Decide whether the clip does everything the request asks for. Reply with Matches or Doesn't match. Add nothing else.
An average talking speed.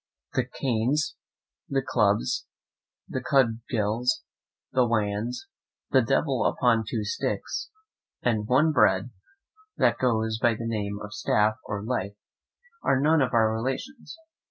Doesn't match